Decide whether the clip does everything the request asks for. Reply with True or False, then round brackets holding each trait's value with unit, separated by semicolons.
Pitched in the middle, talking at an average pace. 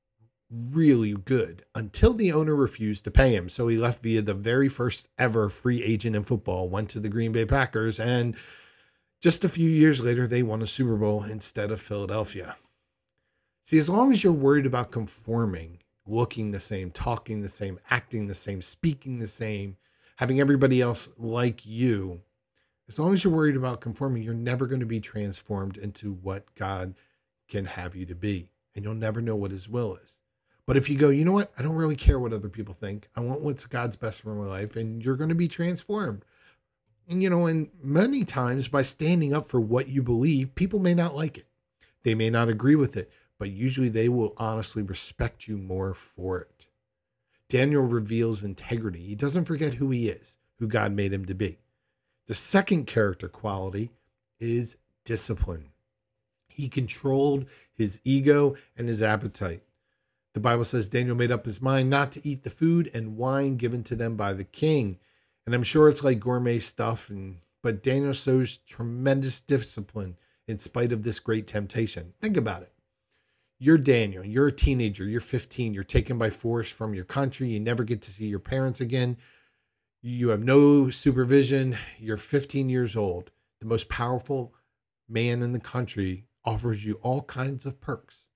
False (115 Hz; 185 wpm)